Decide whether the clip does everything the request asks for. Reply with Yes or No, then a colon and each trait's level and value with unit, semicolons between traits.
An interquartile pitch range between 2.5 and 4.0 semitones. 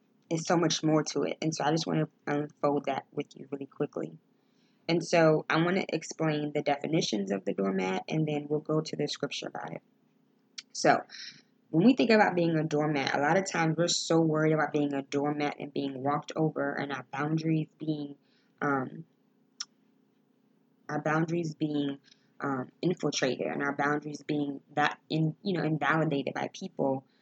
Yes: average, 3.2 semitones